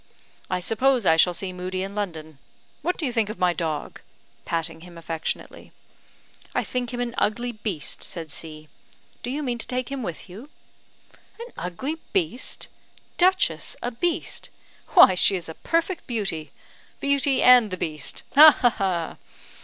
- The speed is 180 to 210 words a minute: No, average, 160 wpm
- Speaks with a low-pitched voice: No, high, 210 Hz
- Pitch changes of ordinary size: No, wide, 6.9 semitones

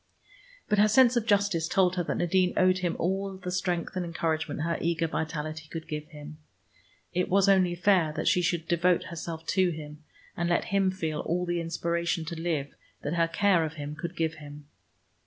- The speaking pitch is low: No, medium, 170 Hz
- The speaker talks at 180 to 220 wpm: Yes, average, 195 wpm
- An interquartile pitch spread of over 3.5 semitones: No, narrow, 2.5 semitones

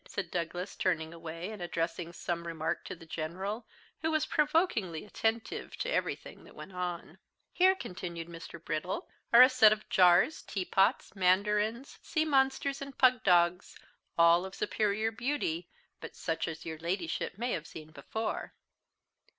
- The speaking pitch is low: No, medium, 185 Hz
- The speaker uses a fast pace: No, average, 150 wpm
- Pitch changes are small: No, average, 5.0 semitones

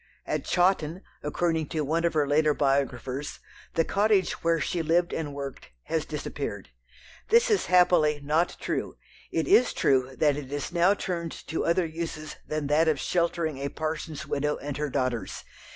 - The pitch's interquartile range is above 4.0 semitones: No, average, 2.9 semitones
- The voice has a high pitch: No, medium, 155 Hz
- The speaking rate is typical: Yes, average, 170 wpm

